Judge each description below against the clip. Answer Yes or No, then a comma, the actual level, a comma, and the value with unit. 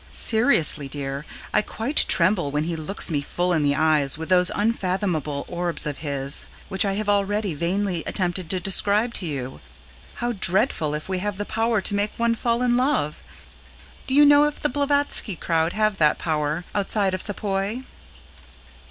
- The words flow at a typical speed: Yes, average, 175 wpm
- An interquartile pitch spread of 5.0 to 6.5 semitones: Yes, average, 5.3 semitones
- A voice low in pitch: No, high, 190 Hz